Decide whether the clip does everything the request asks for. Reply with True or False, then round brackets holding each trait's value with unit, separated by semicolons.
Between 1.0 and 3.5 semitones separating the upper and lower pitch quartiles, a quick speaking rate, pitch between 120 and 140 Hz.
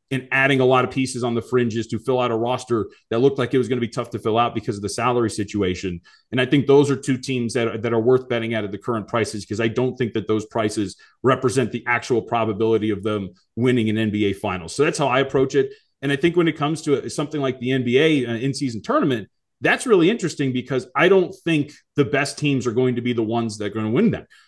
True (3.1 semitones; 265 wpm; 125 Hz)